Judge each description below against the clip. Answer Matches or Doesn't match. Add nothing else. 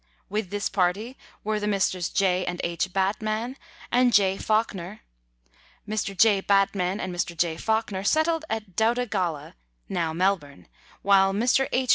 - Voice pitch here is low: Doesn't match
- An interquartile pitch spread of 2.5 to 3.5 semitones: Matches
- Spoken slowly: Doesn't match